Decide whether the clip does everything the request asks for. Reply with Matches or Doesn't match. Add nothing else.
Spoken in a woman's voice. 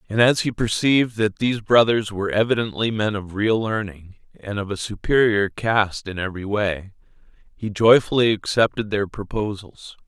Doesn't match